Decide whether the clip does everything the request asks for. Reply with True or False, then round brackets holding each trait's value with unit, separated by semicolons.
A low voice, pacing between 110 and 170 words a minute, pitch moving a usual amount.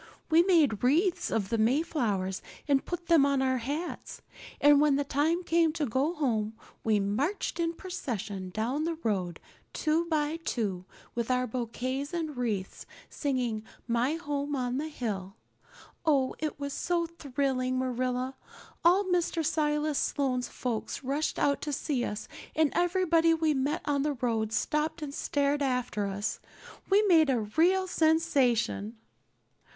False (280 Hz; 150 wpm; 4.8 semitones)